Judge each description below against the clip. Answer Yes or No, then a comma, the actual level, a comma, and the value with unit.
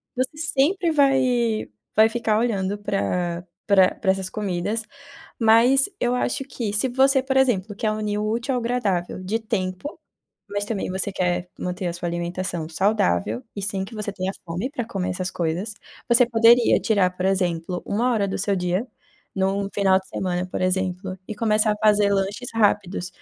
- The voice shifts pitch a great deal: No, average, 3.9 semitones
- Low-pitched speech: No, high, 205 Hz